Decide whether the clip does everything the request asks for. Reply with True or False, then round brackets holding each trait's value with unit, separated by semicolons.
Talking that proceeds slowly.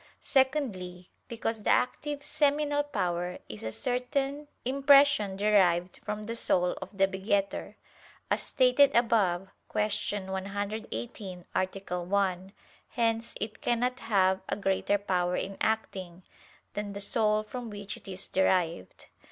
True (125 wpm)